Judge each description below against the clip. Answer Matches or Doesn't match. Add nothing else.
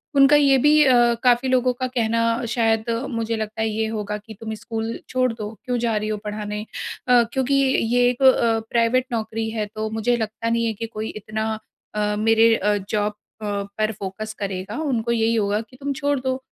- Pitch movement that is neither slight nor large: Doesn't match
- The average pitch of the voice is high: Matches